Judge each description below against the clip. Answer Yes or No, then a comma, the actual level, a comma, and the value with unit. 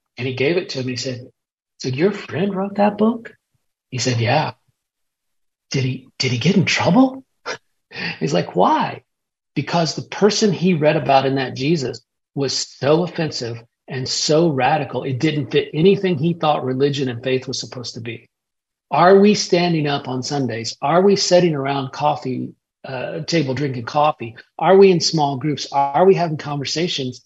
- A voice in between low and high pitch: Yes, medium, 145 Hz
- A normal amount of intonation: Yes, average, 5.0 semitones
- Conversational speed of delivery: Yes, average, 175 wpm